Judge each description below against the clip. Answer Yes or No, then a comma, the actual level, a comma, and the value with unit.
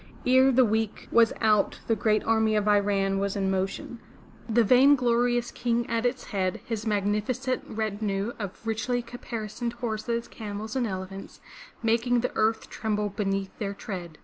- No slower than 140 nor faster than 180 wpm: Yes, average, 150 wpm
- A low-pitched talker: No, high, 220 Hz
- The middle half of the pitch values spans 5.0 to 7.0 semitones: No, average, 2.9 semitones